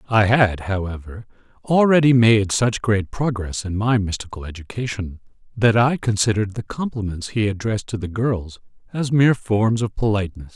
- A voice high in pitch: No, low, 105 Hz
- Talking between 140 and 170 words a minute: Yes, average, 155 wpm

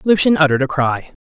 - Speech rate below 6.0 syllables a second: No, 6.7 syllables/s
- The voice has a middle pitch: Yes, medium, 170 Hz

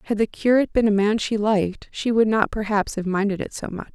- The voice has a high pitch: Yes, high, 210 Hz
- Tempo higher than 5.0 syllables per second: Yes, 6.0 syllables/s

